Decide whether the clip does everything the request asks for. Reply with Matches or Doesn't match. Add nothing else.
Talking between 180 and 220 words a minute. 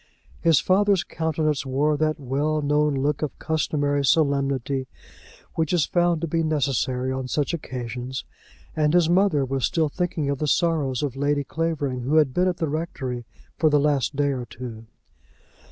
Doesn't match